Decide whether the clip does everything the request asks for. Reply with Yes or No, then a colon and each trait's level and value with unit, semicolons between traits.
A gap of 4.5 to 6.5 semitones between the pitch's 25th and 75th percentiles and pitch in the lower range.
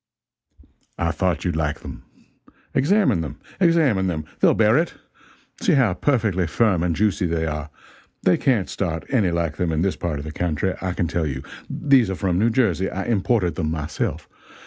Yes: wide, 5.6 semitones; very low, 90 Hz